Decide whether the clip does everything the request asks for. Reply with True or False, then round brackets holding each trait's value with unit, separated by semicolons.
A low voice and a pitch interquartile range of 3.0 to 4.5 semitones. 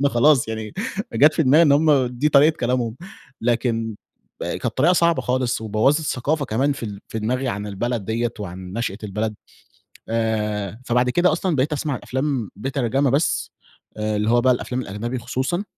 True (125 Hz; 4.1 semitones)